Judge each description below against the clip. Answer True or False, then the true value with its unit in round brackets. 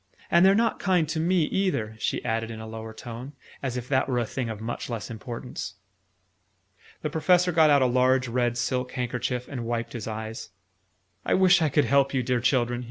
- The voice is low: True (125 Hz)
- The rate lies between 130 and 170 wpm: False (205 wpm)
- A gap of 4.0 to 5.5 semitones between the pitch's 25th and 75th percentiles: True (4.3 semitones)